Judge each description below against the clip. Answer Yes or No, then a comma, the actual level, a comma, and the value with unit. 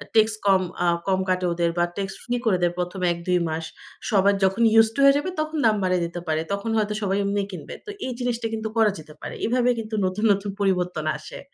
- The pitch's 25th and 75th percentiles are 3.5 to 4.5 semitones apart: Yes, average, 3.8 semitones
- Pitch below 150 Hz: No, high, 195 Hz